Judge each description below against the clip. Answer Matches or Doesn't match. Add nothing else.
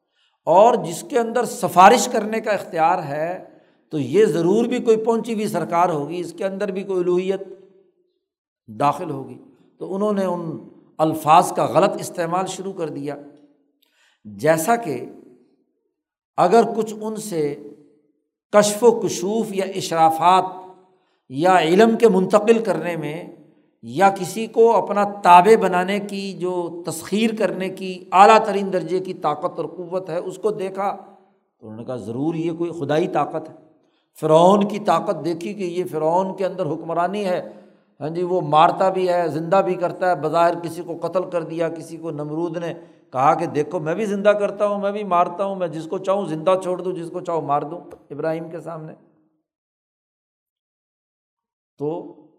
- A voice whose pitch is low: Doesn't match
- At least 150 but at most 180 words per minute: Matches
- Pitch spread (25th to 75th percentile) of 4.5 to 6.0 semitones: Doesn't match